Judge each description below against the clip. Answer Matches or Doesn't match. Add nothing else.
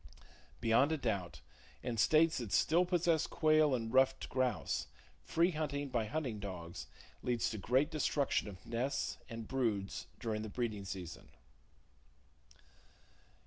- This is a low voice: Matches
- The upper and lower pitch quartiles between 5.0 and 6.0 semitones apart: Matches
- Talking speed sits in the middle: Doesn't match